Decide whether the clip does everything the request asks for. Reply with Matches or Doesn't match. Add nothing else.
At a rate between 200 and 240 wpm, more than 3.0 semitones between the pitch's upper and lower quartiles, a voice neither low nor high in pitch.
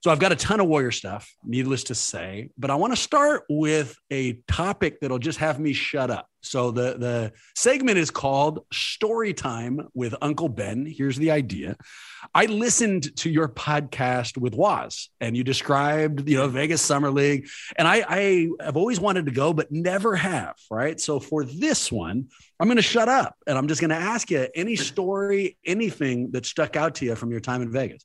Matches